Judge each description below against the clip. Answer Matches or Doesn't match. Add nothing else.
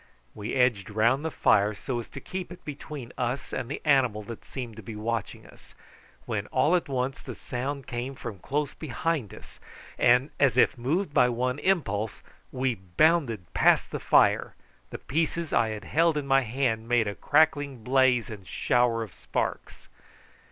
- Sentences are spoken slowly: Doesn't match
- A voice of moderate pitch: Doesn't match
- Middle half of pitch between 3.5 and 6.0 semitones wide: Matches